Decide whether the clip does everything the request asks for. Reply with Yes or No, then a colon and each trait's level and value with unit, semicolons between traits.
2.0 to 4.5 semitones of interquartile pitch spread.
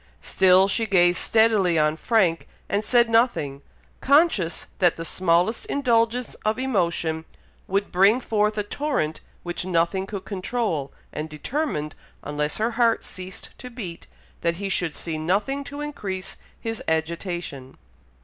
No: average, 5.3 semitones